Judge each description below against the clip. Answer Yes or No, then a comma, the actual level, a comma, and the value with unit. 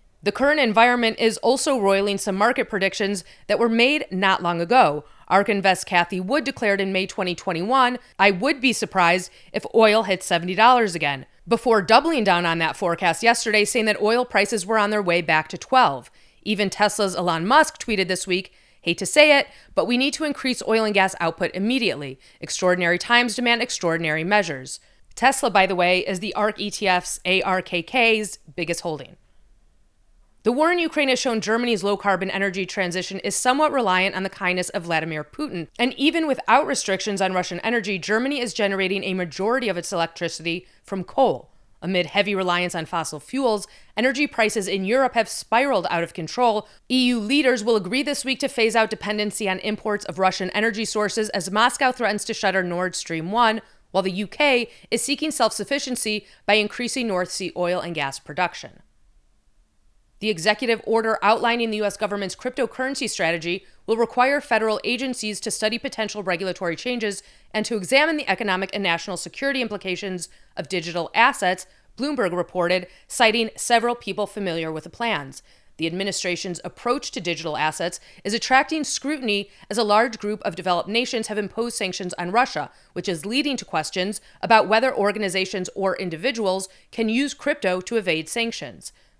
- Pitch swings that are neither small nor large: Yes, average, 4.5 semitones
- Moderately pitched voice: No, high, 205 Hz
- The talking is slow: No, average, 170 wpm